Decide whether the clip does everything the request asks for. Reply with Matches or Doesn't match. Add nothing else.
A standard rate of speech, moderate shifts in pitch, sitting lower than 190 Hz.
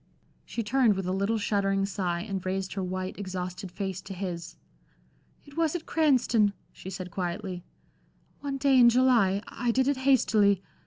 Doesn't match